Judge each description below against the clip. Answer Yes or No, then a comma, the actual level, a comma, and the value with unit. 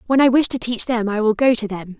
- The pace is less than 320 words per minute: No, fast, 330 wpm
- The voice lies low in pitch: No, high, 230 Hz